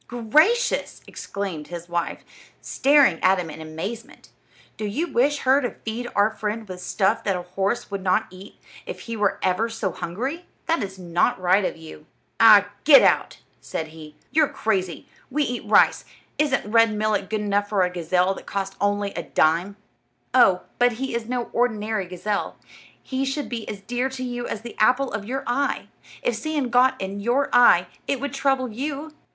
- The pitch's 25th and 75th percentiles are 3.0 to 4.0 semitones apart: No, average, 5.1 semitones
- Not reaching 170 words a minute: No, average, 185 wpm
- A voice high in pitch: Yes, high, 215 Hz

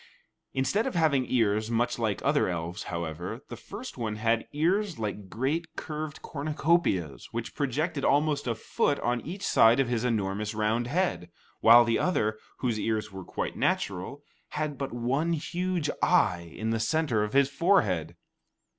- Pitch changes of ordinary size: No, wide, 6.1 semitones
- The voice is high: No, low, 120 Hz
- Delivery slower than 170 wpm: Yes, average, 160 wpm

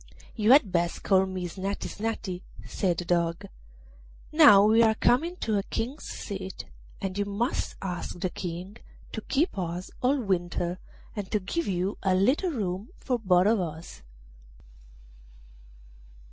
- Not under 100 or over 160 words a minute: Yes, average, 145 wpm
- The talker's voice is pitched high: Yes, high, 195 Hz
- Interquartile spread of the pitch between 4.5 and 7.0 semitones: No, average, 3.9 semitones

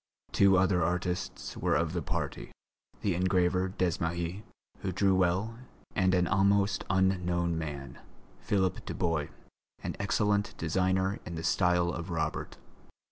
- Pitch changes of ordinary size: No, narrow, 1.8 semitones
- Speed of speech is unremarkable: No, slow, 130 wpm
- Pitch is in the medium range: No, very low, 90 Hz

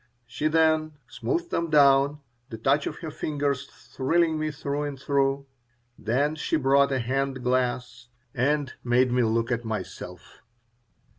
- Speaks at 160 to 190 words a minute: No, average, 145 wpm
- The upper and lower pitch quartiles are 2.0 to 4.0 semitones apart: Yes, average, 3.1 semitones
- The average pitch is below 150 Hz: Yes, medium, 140 Hz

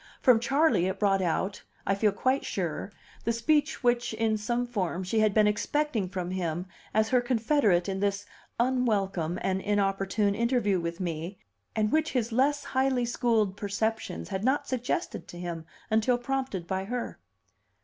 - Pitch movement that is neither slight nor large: Yes, average, 4.3 semitones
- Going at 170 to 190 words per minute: No, average, 160 wpm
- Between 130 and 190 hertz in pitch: No, high, 215 Hz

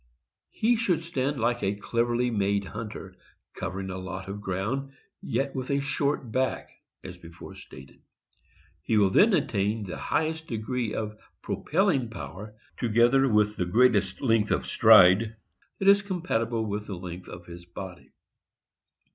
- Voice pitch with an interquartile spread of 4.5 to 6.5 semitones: Yes, wide, 5.6 semitones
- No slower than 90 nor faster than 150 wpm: Yes, average, 145 wpm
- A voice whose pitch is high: No, low, 110 Hz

